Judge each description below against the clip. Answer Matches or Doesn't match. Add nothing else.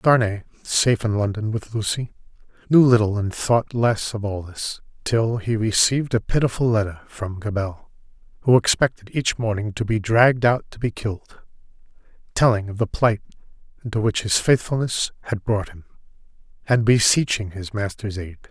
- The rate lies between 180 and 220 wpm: Doesn't match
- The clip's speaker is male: Matches